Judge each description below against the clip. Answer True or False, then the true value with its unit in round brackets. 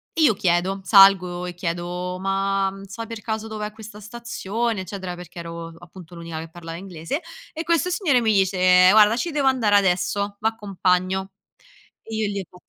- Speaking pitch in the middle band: False (195 Hz)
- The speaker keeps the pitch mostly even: False (3.5 semitones)